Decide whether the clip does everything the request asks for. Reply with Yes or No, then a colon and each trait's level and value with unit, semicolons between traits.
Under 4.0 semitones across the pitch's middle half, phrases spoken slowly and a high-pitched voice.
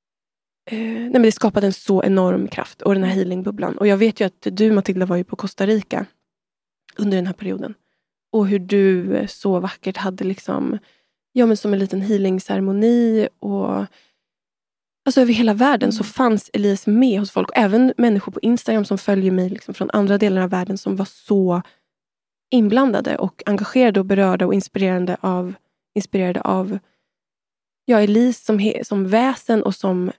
No: average, 2.7 semitones; average, 175 wpm; high, 200 Hz